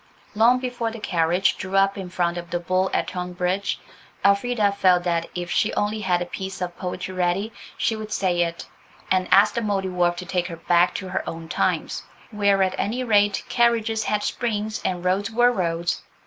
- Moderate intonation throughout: Yes, average, 3.0 semitones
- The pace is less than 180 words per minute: No, average, 190 wpm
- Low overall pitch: No, high, 190 Hz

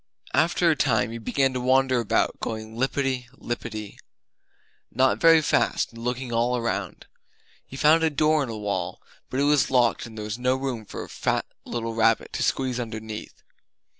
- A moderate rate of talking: Yes, average, 180 wpm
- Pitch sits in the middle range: No, low, 125 Hz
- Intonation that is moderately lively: Yes, average, 3.1 semitones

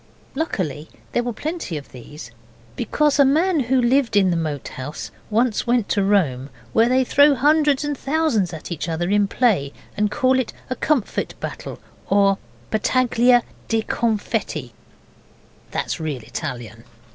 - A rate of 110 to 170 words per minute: Yes, average, 150 wpm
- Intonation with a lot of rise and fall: Yes, wide, 8.1 semitones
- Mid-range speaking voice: No, high, 220 Hz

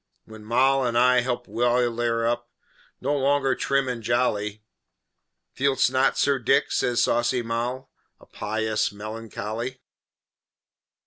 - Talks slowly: Yes, slow, 120 wpm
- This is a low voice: Yes, low, 120 Hz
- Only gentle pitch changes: Yes, narrow, 2.3 semitones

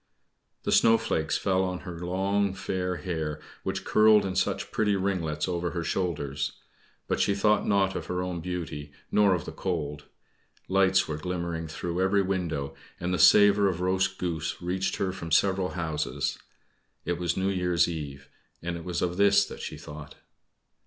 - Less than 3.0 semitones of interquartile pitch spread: Yes, narrow, 2.6 semitones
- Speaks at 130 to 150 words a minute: No, average, 170 wpm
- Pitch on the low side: Yes, very low, 90 Hz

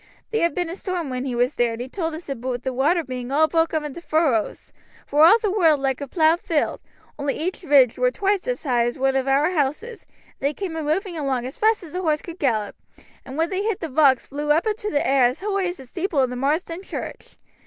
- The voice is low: No, very high, 305 Hz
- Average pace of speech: No, fast, 250 wpm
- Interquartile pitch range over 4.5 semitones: Yes, average, 5.0 semitones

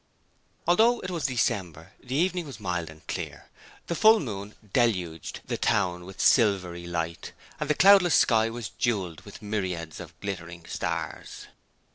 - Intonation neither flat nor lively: No, wide, 7.7 semitones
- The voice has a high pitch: No, low, 100 Hz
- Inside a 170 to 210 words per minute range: No, average, 150 wpm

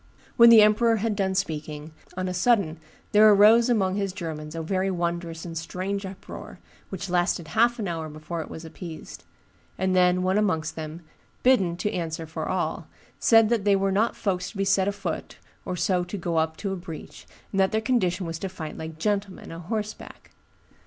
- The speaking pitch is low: No, medium, 185 Hz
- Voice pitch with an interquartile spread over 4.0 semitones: No, average, 3.6 semitones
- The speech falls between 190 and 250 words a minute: Yes, average, 195 wpm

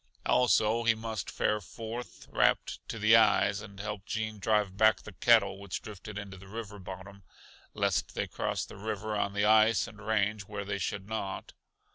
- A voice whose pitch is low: Yes, low, 105 Hz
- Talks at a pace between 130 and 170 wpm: No, average, 180 wpm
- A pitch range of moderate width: No, narrow, 1.7 semitones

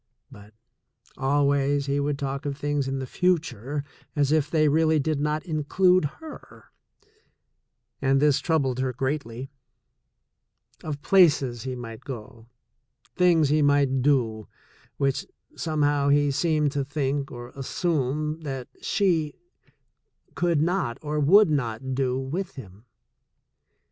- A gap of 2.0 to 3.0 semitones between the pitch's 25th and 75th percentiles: Yes, narrow, 2.6 semitones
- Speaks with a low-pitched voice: No, medium, 145 Hz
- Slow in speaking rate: Yes, slow, 130 wpm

